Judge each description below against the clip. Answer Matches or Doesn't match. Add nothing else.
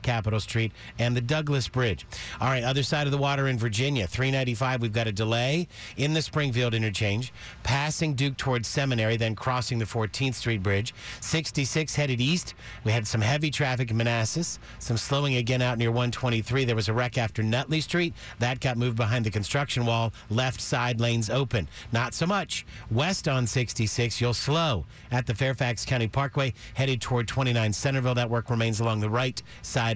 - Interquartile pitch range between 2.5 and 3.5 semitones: Matches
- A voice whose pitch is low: Matches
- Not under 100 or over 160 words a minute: Doesn't match